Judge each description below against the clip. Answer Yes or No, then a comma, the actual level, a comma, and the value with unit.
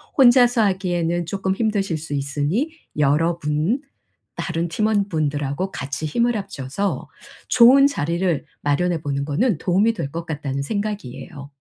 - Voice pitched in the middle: Yes, medium, 170 Hz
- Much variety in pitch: Yes, wide, 5.9 semitones